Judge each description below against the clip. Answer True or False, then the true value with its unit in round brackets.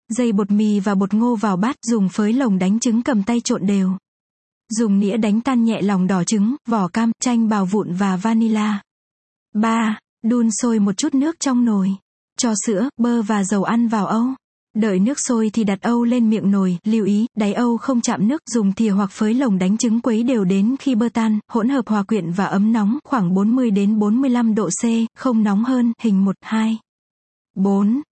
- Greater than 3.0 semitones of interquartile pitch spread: False (2.6 semitones)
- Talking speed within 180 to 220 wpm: True (205 wpm)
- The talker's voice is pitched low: False (220 Hz)